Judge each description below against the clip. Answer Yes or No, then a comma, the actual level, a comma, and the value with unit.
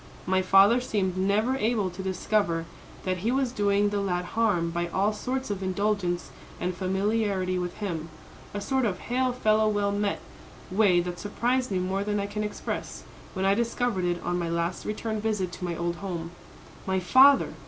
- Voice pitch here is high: Yes, high, 200 Hz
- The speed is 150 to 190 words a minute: Yes, average, 185 wpm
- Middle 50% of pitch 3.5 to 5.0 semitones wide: No, average, 3.0 semitones